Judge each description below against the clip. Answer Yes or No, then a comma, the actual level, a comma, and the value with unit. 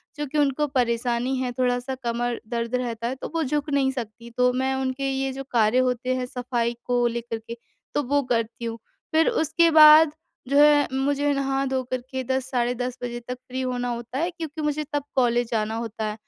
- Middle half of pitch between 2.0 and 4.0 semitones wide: Yes, average, 2.9 semitones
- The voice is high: Yes, very high, 255 Hz